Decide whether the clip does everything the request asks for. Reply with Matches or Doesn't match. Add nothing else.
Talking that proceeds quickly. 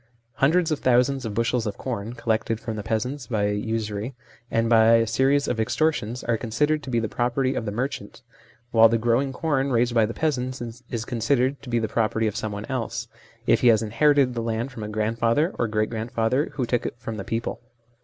Matches